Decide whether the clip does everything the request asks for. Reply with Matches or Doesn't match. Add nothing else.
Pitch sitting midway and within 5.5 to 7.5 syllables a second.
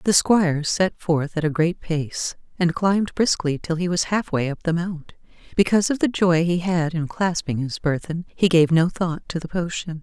Doesn't match